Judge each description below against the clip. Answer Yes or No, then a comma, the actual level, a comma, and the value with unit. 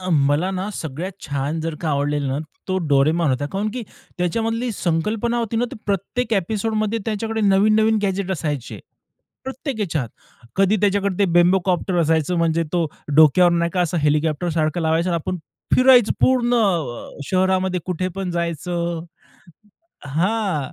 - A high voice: No, medium, 180 Hz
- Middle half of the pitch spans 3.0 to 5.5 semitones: Yes, average, 4.4 semitones